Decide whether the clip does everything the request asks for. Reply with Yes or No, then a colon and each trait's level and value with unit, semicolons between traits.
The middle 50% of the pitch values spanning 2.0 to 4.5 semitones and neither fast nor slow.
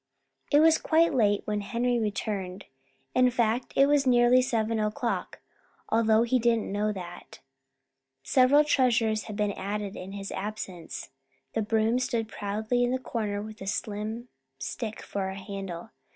Yes: average, 3.1 semitones; average, 150 wpm